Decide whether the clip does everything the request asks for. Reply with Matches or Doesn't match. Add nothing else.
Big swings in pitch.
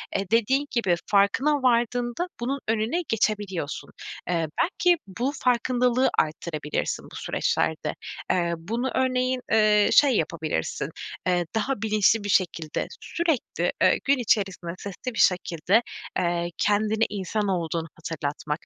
Matches